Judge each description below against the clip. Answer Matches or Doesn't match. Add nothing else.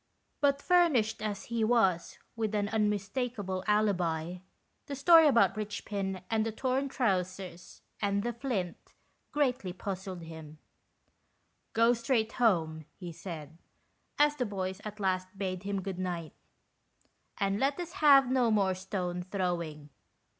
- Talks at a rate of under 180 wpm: Matches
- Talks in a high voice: Matches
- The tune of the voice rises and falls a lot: Doesn't match